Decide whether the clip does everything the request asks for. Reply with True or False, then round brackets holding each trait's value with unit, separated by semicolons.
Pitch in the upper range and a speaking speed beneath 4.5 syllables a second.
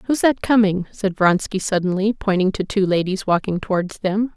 False (195 Hz; 4.9 syllables/s)